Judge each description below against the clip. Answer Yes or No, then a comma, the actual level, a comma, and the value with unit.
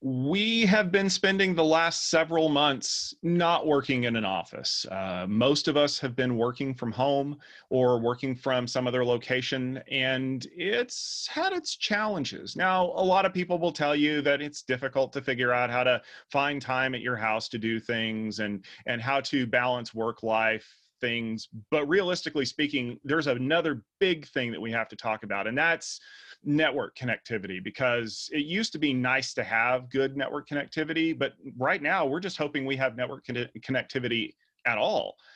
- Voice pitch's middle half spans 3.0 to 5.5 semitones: Yes, average, 4.5 semitones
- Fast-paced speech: No, average, 180 wpm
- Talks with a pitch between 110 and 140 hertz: Yes, low, 135 Hz